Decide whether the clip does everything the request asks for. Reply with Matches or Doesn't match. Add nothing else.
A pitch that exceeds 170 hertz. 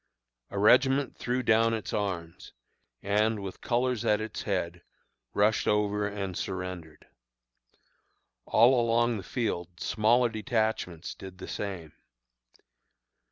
Doesn't match